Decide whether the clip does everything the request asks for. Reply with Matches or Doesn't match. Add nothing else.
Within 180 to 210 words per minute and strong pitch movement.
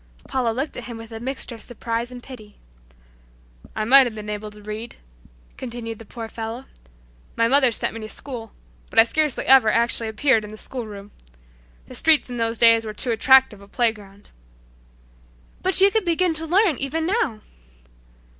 Doesn't match